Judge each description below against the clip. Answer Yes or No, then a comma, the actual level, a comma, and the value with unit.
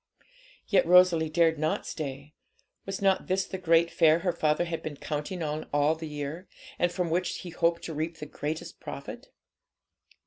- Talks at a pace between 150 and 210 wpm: Yes, average, 175 wpm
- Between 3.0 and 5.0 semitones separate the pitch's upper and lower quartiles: No, narrow, 2.5 semitones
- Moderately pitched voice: Yes, medium, 165 Hz